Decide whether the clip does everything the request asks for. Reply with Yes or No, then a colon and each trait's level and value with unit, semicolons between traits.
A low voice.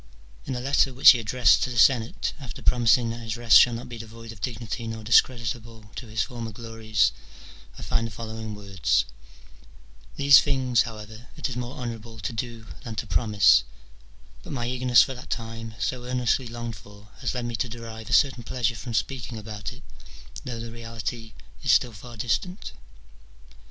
Yes: low, 115 Hz